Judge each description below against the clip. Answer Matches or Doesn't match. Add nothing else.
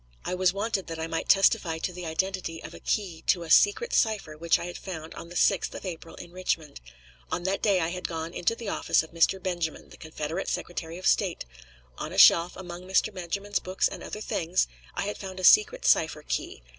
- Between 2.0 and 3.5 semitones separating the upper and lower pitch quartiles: Matches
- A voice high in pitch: Doesn't match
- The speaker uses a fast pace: Matches